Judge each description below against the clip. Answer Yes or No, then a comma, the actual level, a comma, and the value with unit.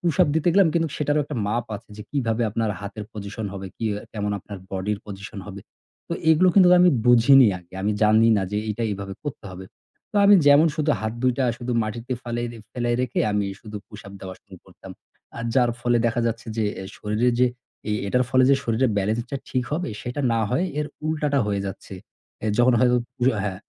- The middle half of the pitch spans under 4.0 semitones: No, average, 4.4 semitones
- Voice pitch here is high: No, low, 115 Hz